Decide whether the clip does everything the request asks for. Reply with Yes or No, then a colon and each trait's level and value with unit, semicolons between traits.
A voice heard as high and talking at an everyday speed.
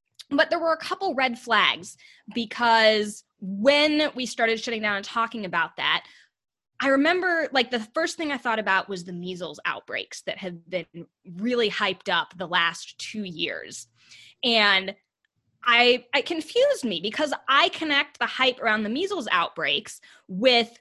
Yes: high, 235 Hz; average, 160 wpm